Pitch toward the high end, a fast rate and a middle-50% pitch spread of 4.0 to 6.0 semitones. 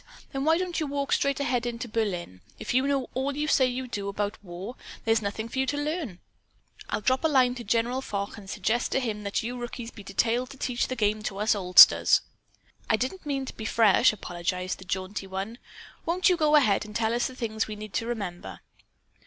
Yes: high, 230 Hz; fast, 225 wpm; average, 4.4 semitones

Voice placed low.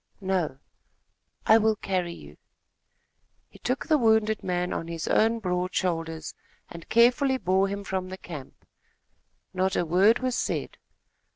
No: high, 190 Hz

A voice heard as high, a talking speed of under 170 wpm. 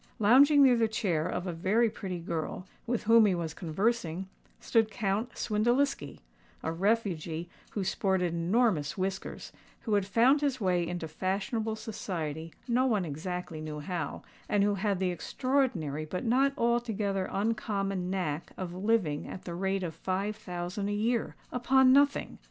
Yes: high, 195 Hz; average, 150 wpm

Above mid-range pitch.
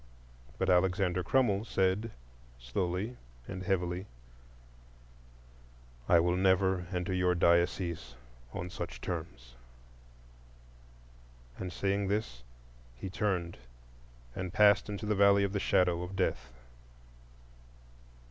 No: very low, 95 Hz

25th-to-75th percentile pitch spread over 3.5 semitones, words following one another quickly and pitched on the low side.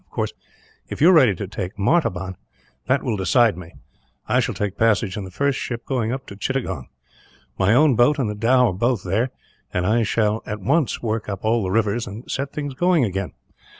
Yes: average, 4.8 semitones; fast, 220 wpm; low, 110 Hz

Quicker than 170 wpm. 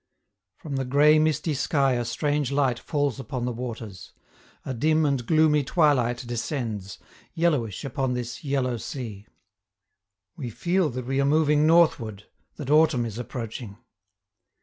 No: average, 140 wpm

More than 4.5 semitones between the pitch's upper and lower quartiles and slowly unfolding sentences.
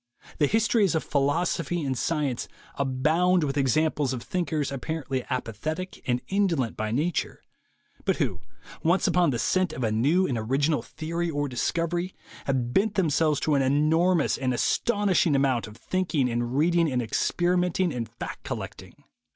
No: average, 5.0 semitones; average, 155 wpm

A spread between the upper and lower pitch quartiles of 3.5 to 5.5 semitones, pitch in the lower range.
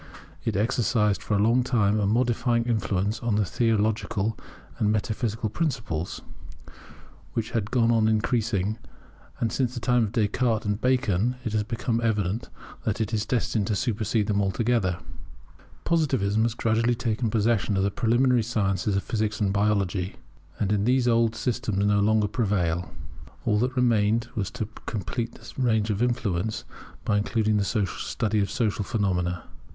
No: narrow, 2.5 semitones; low, 110 Hz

